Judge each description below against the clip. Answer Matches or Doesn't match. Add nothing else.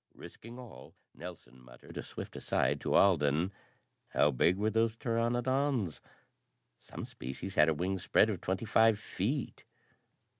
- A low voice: Matches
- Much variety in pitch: Matches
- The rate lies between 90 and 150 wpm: Matches